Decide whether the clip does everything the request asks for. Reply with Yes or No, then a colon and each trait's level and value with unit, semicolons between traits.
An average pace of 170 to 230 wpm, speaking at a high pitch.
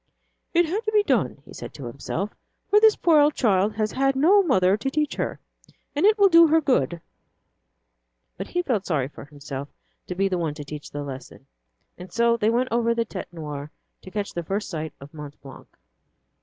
Yes: fast, 205 wpm; high, 205 Hz